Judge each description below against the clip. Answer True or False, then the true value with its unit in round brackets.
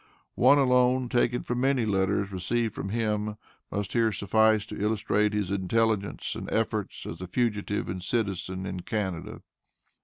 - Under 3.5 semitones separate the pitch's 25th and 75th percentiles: True (2.9 semitones)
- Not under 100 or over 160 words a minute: True (150 wpm)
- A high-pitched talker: False (105 Hz)